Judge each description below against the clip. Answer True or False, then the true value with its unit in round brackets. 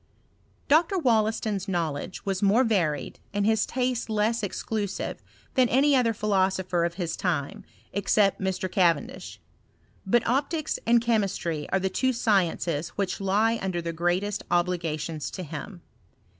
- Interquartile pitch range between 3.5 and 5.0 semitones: True (4.5 semitones)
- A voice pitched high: True (195 Hz)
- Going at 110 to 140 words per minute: True (135 wpm)